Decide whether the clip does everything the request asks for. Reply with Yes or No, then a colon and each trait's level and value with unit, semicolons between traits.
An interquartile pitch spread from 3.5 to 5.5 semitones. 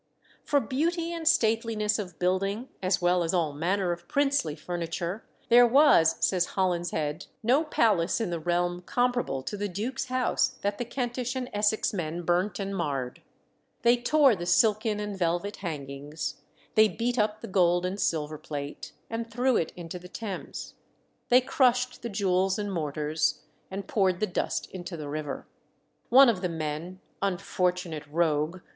Yes: average, 5.1 semitones